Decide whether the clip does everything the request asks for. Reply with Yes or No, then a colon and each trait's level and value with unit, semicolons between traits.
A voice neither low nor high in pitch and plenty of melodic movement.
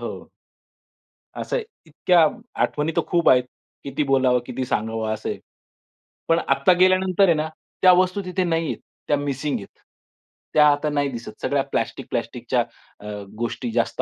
Yes: medium, 145 Hz; wide, 5.7 semitones